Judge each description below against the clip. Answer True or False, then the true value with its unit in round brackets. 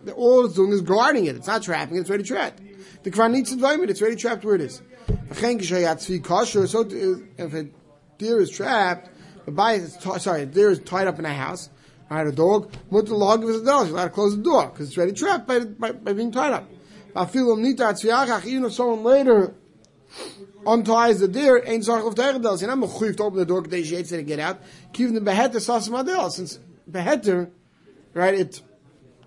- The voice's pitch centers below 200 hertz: False (205 Hz)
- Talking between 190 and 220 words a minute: True (200 wpm)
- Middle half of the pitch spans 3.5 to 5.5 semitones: True (4.7 semitones)